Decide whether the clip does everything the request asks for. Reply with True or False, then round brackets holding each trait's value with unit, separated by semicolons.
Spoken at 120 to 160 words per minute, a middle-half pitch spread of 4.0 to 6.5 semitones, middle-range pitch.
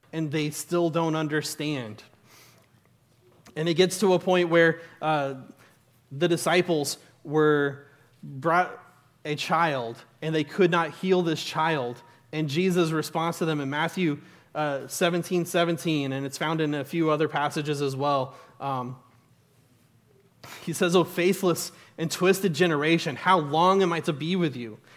False (150 wpm; 3.5 semitones; 155 Hz)